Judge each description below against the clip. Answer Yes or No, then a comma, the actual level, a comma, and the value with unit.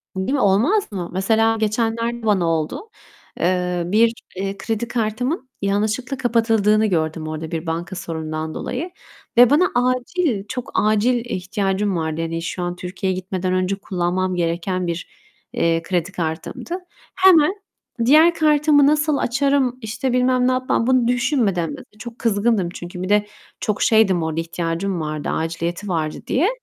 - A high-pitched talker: Yes, high, 205 Hz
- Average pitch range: No, wide, 5.9 semitones